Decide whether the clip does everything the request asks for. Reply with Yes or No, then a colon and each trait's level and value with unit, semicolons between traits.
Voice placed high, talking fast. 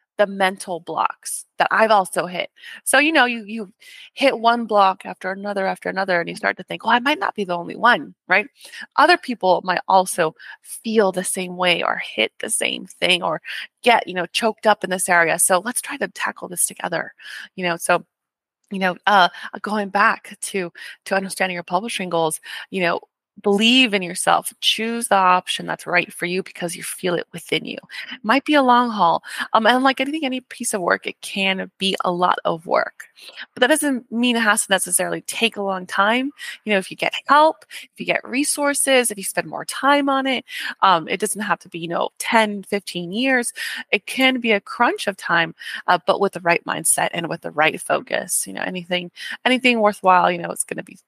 Yes: high, 200 Hz; fast, 215 wpm